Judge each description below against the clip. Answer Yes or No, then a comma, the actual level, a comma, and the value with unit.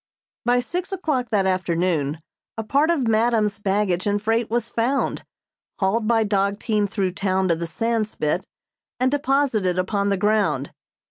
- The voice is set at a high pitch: Yes, high, 210 Hz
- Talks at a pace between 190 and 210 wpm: No, average, 150 wpm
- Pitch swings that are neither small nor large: Yes, average, 3.9 semitones